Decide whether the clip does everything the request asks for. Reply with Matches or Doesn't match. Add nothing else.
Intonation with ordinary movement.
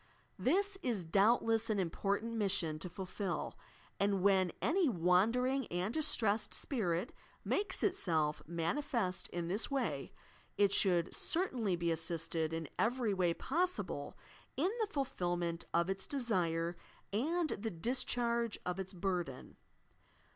Doesn't match